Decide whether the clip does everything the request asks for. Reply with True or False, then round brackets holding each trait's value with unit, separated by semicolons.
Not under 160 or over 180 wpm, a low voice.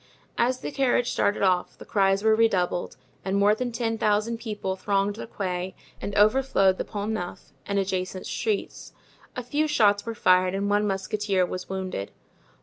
False (170 wpm; 205 Hz)